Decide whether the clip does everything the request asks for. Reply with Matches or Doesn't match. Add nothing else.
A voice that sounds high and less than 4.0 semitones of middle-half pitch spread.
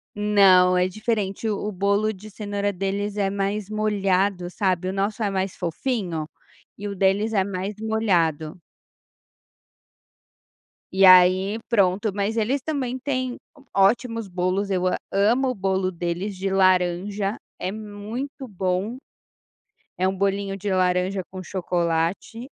Matches